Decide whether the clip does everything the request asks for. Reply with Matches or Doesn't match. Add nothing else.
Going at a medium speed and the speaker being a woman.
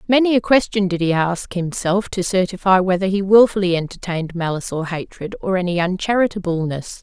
Matches